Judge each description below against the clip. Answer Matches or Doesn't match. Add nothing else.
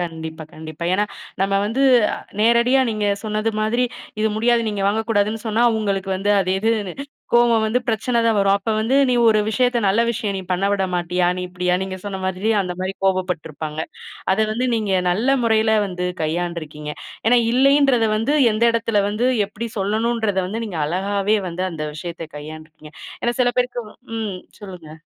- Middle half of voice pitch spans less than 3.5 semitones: Doesn't match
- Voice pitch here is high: Matches